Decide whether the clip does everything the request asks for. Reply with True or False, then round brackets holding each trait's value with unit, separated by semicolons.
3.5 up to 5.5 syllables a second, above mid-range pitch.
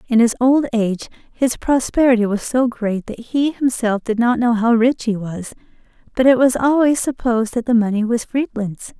True (5.0 syllables/s; 240 Hz)